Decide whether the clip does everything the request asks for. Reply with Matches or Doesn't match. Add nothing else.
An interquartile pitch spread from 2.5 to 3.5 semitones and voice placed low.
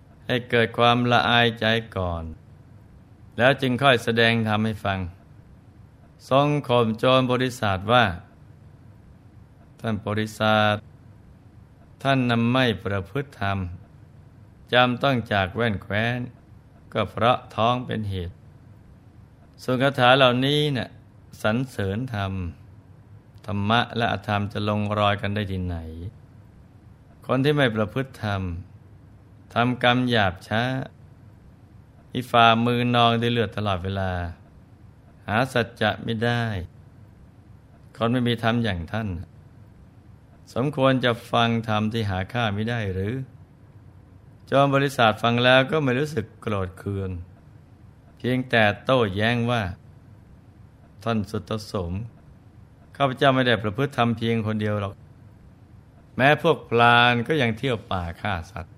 Matches